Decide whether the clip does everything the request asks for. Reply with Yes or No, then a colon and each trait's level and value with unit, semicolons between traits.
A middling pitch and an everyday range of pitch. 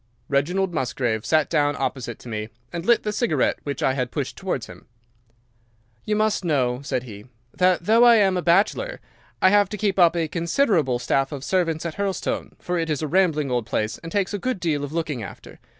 No: medium, 165 Hz; wide, 6.0 semitones